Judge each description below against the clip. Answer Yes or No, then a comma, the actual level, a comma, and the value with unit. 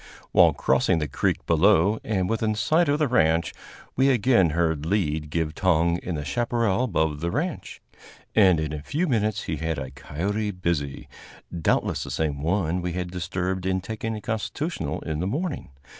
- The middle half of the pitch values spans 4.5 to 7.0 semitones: Yes, wide, 5.4 semitones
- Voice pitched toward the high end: No, very low, 90 Hz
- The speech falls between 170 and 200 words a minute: Yes, average, 175 wpm